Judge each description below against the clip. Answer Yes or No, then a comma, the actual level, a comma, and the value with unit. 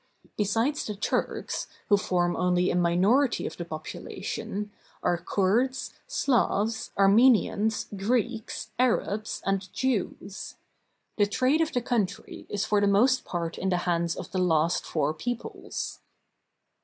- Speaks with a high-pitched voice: Yes, high, 205 Hz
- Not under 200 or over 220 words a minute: No, slow, 135 wpm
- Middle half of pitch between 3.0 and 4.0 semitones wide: No, average, 4.8 semitones